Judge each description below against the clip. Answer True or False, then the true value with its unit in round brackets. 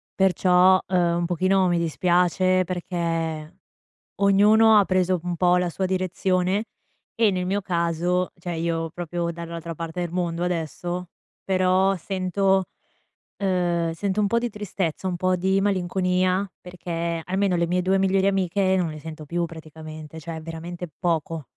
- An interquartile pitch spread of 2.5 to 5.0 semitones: False (1.9 semitones)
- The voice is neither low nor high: True (180 Hz)